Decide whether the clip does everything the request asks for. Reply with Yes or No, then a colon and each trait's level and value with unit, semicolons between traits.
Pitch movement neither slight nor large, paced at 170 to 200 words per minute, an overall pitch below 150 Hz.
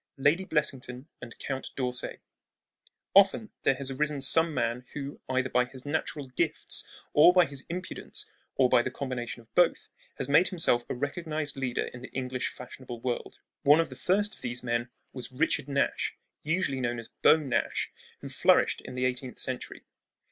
Yes: average, 3.2 semitones; average, 175 wpm; low, 135 Hz